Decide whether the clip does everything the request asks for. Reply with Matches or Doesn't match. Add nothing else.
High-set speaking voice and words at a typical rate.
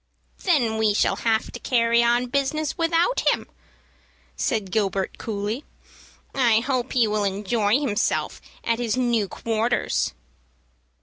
Doesn't match